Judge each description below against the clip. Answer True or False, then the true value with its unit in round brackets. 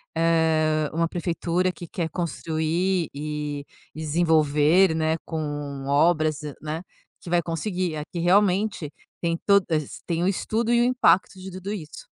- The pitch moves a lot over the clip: False (2.8 semitones)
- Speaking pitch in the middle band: True (165 Hz)